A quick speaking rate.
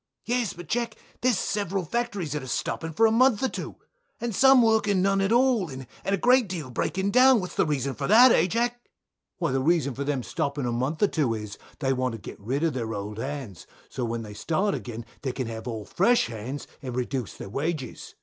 Yes: fast, 230 wpm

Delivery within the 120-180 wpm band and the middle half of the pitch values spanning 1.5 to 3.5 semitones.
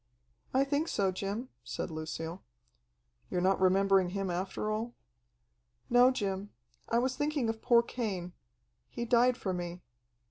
No: average, 140 wpm; average, 4.7 semitones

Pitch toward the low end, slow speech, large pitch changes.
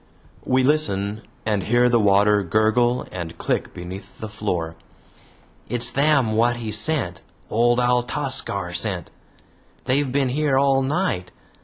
No: low, 115 Hz; slow, 130 wpm; average, 4.8 semitones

